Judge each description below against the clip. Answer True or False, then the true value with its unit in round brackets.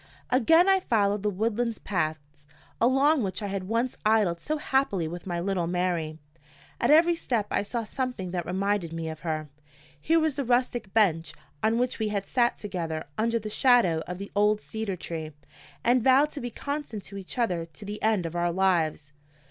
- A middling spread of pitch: False (5.7 semitones)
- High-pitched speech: True (205 Hz)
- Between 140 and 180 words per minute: False (190 wpm)